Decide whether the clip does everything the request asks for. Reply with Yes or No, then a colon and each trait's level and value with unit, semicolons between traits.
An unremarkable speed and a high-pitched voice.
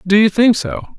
No: fast, 245 wpm; high, 205 Hz